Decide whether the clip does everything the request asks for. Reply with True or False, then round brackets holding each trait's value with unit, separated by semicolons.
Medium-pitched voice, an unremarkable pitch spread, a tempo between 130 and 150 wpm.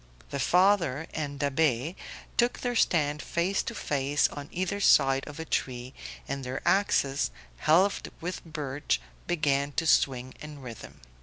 True (145 Hz; 4.1 semitones; 145 wpm)